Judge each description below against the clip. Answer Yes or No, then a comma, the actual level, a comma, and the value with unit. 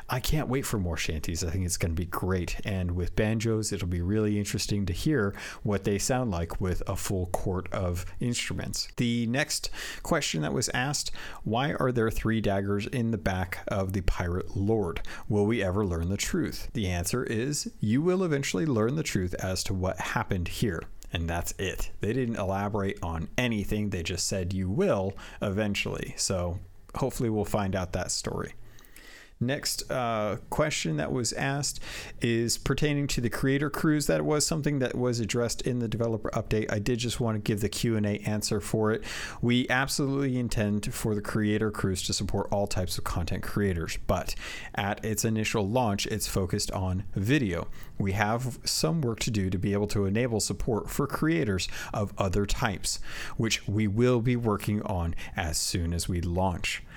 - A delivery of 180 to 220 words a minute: Yes, average, 185 wpm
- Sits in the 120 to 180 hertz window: No, low, 105 Hz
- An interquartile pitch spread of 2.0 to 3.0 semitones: No, average, 3.8 semitones